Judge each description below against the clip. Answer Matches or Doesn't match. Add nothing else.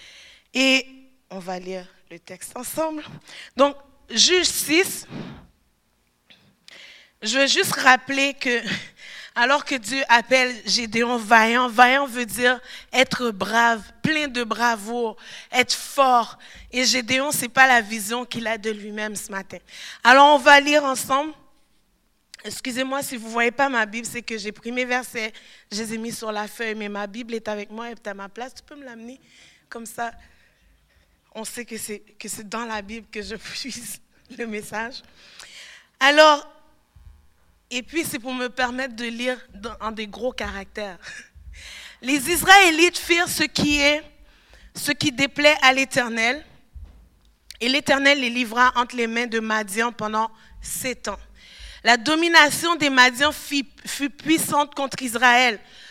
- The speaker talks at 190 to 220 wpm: Doesn't match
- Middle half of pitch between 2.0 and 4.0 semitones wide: Matches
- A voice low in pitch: Doesn't match